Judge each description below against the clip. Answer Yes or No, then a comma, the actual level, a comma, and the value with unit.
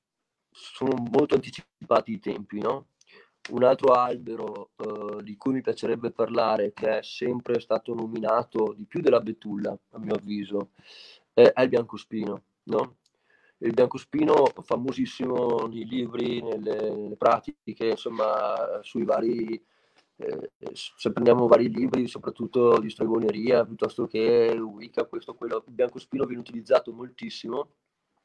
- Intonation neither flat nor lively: Yes, average, 3.1 semitones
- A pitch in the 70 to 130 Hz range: Yes, low, 120 Hz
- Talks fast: No, average, 125 wpm